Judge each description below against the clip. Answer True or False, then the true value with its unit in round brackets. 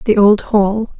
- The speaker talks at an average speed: True (180 wpm)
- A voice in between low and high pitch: False (210 Hz)